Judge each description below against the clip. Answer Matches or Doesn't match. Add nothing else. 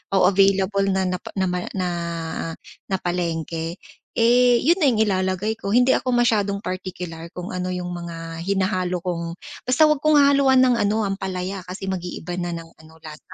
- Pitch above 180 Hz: Matches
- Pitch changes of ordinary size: Matches